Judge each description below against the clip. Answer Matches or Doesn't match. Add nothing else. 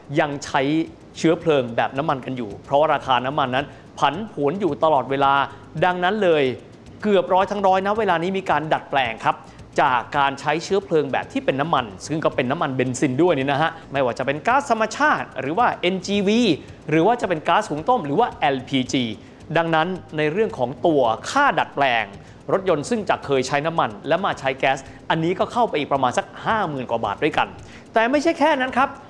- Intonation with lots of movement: Matches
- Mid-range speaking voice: Matches